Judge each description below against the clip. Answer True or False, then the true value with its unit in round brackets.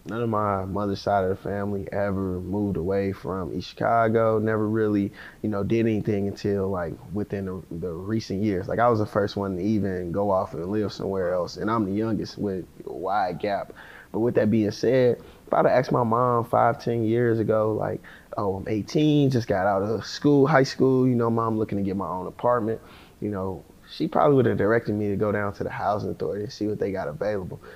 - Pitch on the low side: True (105 Hz)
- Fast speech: True (225 wpm)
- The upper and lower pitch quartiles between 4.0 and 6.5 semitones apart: False (2.4 semitones)